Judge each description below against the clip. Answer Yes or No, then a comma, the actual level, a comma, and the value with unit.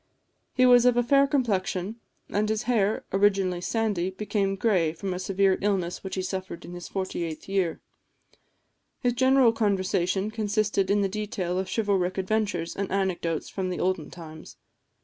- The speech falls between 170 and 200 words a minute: No, average, 160 wpm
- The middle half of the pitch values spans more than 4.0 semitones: No, average, 2.7 semitones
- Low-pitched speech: No, high, 195 Hz